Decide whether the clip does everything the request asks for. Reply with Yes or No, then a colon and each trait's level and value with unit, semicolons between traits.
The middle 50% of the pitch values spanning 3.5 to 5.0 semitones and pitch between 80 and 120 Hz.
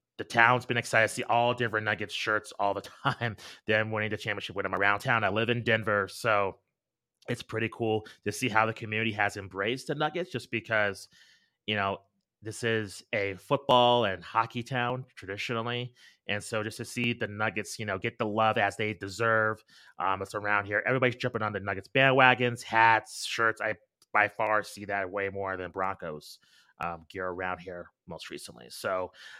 No: average, 2.8 semitones; low, 110 Hz